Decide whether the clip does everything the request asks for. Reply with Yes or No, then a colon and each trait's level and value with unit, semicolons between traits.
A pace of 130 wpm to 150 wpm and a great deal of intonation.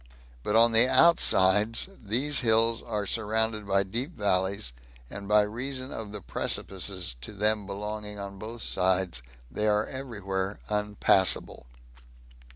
No: slow, 135 wpm; narrow, 2.5 semitones